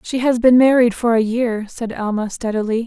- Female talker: Yes, female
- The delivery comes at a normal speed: No, fast, 210 wpm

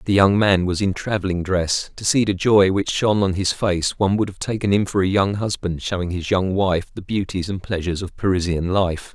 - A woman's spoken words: No, male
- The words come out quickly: Yes, fast, 235 wpm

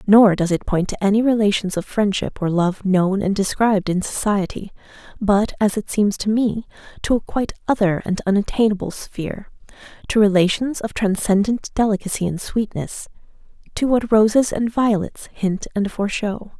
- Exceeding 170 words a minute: No, average, 160 wpm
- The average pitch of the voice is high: Yes, high, 205 Hz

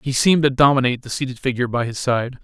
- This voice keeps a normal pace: No, fast, 245 wpm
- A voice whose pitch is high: No, low, 130 Hz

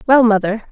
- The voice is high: Yes, high, 225 Hz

